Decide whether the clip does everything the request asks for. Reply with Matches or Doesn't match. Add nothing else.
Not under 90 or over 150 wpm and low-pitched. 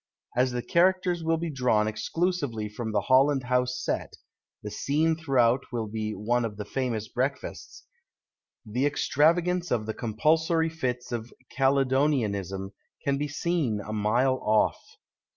Matches